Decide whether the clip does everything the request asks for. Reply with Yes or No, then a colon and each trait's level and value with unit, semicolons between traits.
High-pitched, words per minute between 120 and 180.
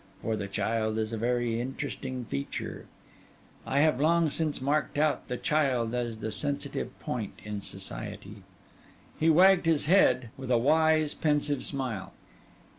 No: low, 130 Hz; average, 145 wpm